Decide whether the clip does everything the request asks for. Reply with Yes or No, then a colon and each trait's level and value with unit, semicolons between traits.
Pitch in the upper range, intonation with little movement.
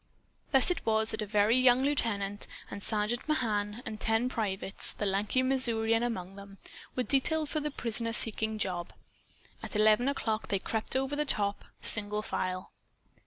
No: high, 220 Hz; average, 3.7 semitones